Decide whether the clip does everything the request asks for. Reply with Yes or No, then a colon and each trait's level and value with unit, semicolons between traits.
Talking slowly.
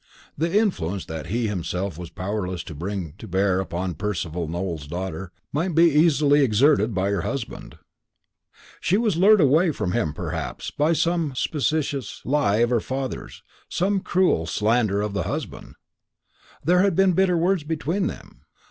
No: average, 155 wpm